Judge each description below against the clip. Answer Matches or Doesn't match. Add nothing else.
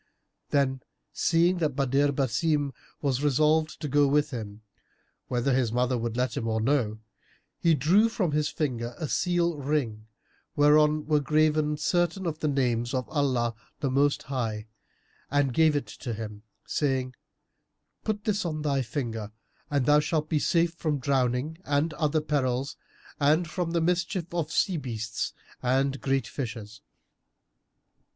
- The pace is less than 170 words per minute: Matches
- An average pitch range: Matches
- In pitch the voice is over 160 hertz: Doesn't match